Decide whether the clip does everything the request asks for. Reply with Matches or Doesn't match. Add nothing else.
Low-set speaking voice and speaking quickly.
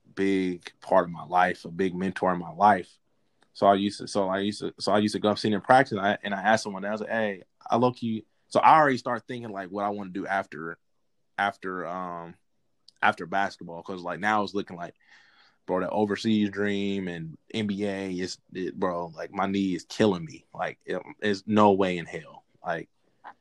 Matches